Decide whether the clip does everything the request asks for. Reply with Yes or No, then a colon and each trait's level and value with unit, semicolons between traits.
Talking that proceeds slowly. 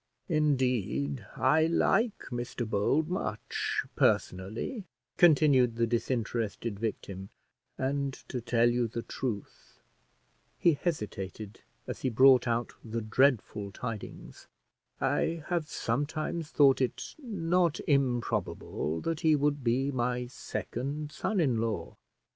Yes: slow, 115 wpm